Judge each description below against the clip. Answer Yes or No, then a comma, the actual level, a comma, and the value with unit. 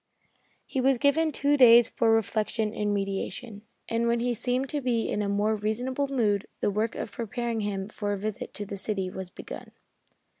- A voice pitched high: Yes, high, 225 Hz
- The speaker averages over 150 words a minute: Yes, average, 190 wpm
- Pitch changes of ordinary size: Yes, average, 3.2 semitones